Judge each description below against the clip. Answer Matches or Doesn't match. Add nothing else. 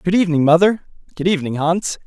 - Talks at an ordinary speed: Matches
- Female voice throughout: Doesn't match